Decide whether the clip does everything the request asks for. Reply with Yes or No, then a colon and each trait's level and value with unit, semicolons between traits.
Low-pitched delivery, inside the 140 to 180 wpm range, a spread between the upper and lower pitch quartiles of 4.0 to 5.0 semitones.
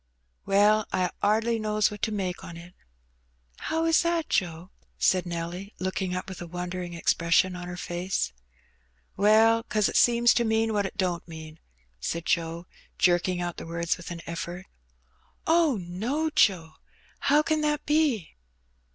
No: medium, 185 Hz; average, 160 wpm; average, 4.4 semitones